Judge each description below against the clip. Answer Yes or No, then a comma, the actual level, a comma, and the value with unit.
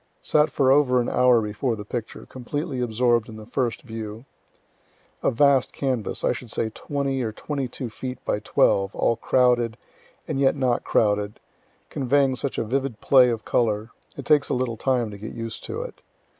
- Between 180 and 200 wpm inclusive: Yes, average, 185 wpm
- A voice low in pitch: Yes, low, 125 Hz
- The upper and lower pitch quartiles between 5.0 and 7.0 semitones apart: No, average, 3.1 semitones